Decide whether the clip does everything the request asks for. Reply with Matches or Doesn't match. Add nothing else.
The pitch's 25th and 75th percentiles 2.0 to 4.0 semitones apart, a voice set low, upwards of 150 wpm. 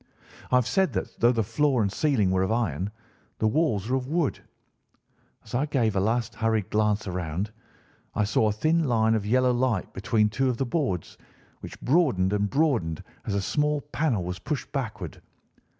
Doesn't match